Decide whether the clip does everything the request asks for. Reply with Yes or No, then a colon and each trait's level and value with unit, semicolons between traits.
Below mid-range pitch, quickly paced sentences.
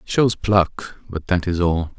Yes: very low, 90 Hz; fast, 210 wpm